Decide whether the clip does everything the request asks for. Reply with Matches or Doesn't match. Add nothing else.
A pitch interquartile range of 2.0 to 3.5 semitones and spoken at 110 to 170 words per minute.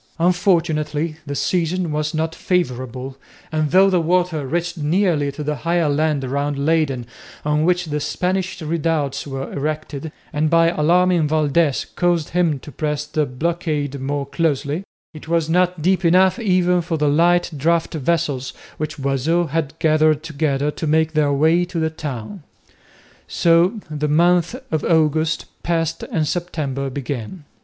Matches